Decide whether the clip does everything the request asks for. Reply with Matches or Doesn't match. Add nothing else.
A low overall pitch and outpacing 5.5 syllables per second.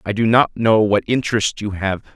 Matches